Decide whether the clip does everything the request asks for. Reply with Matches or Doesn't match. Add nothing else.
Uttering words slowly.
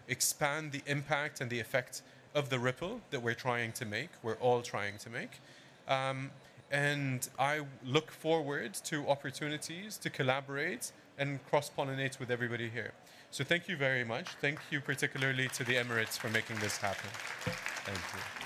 Doesn't match